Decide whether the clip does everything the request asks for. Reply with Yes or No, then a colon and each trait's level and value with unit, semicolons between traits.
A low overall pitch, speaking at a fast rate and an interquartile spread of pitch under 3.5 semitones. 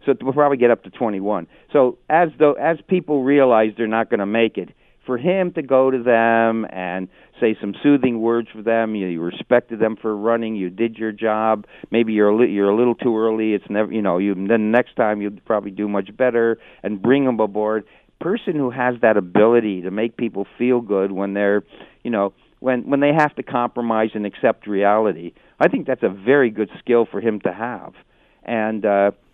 Yes: low, 115 Hz; fast, 215 wpm; average, 3.0 semitones